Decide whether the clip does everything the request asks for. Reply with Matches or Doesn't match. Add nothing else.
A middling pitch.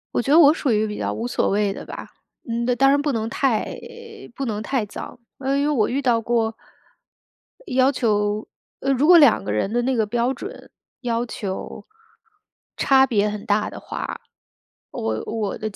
Doesn't match